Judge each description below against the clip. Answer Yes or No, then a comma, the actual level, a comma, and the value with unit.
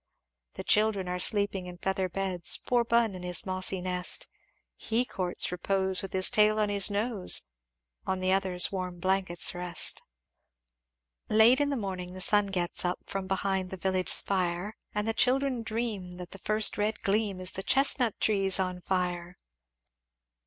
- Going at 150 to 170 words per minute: Yes, average, 165 wpm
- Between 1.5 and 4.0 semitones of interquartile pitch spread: Yes, average, 2.7 semitones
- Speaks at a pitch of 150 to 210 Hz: Yes, high, 190 Hz